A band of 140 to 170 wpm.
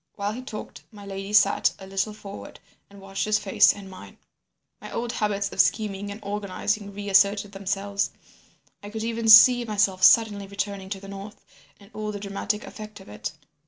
No: average, 180 wpm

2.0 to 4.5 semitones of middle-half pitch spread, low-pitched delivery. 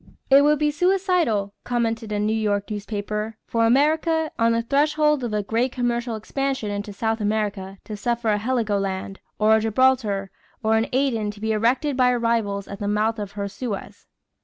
No: average, 3.7 semitones; high, 225 Hz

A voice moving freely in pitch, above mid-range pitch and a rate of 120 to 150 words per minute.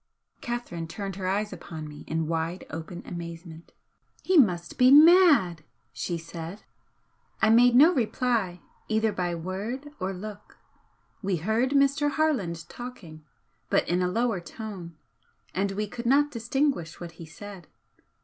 Yes: wide, 6.3 semitones; high, 195 Hz; average, 140 wpm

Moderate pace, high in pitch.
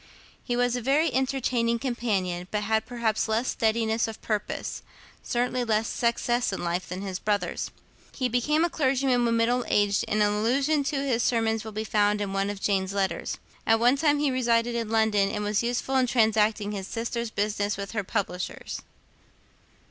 Yes: average, 180 wpm; high, 225 Hz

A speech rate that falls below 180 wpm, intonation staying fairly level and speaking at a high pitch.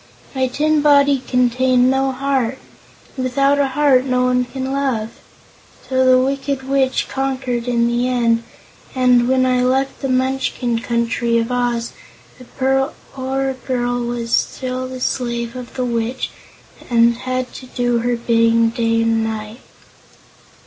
Yes: average, 145 wpm; narrow, 1.9 semitones; very high, 255 Hz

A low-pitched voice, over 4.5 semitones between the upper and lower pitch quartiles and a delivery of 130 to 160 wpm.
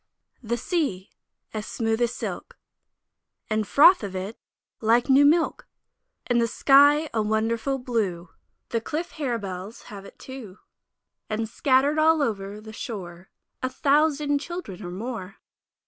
No: high, 230 Hz; average, 5.2 semitones; average, 140 wpm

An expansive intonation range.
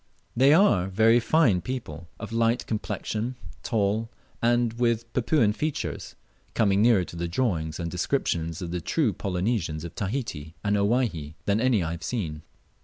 Yes: wide, 5.7 semitones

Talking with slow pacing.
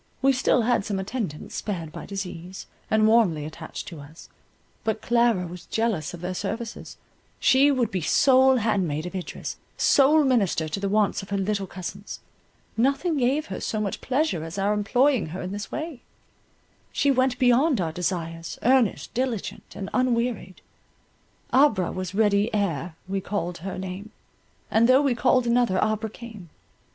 No: average, 165 wpm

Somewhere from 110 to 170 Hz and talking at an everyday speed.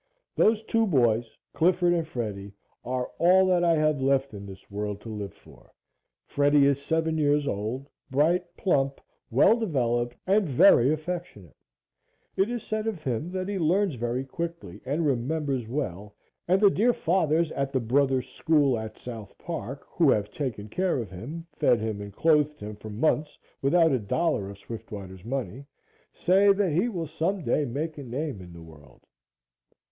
Yes: medium, 140 Hz; average, 170 wpm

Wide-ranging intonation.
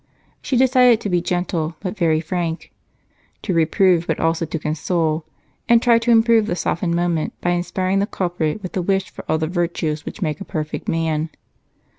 No: average, 3.3 semitones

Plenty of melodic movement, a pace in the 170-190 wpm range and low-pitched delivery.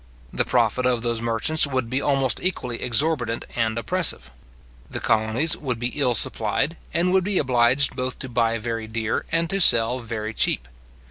No: average, 3.7 semitones; average, 175 wpm; low, 120 Hz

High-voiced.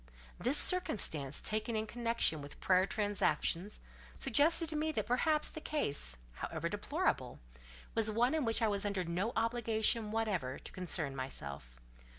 Yes: high, 215 Hz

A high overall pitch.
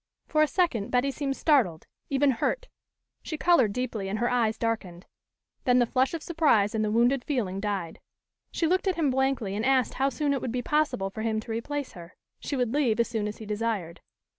Yes: high, 245 Hz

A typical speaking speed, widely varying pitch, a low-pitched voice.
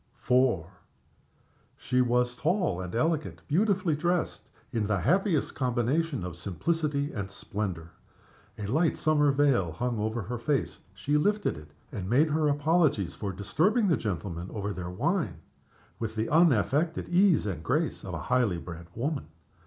Yes: average, 150 wpm; wide, 8.0 semitones; low, 125 Hz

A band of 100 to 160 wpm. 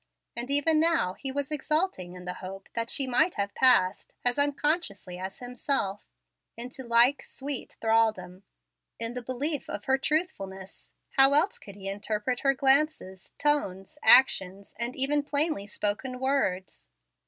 Yes: average, 145 wpm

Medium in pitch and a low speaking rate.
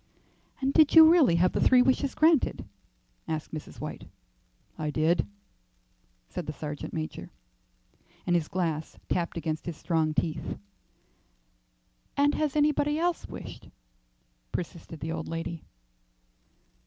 Yes: medium, 170 Hz; slow, 125 wpm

